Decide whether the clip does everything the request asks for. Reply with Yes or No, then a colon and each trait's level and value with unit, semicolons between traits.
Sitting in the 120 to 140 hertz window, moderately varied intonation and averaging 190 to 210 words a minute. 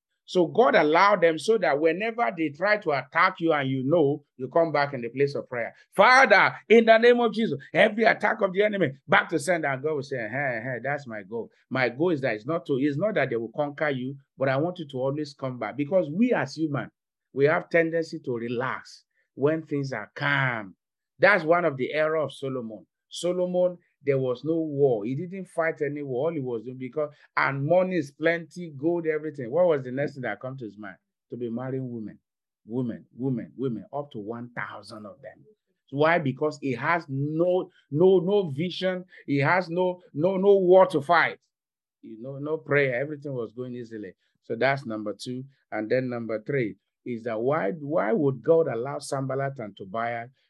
No: medium, 150 Hz; average, 4.9 semitones; fast, 205 wpm